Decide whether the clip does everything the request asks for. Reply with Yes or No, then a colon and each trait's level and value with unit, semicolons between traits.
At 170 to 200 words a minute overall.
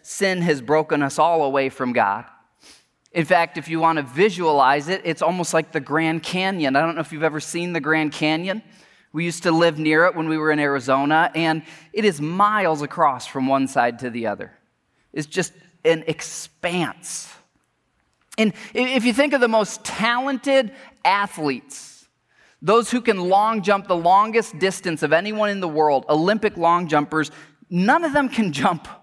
Yes: average, 180 wpm